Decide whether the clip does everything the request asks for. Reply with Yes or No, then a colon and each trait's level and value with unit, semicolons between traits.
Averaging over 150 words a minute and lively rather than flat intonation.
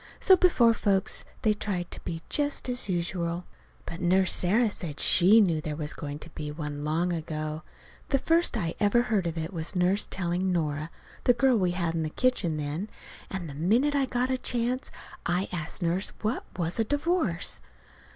Yes: average, 190 wpm; wide, 5.8 semitones